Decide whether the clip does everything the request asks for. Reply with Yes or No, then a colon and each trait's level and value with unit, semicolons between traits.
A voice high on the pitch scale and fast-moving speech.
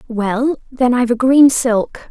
No: high, 245 Hz; average, 170 wpm